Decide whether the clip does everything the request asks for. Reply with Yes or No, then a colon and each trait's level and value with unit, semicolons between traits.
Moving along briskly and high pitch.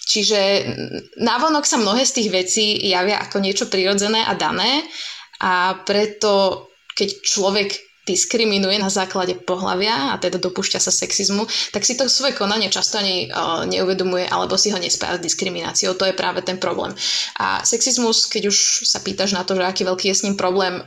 Yes: fast, 175 wpm; high, 200 Hz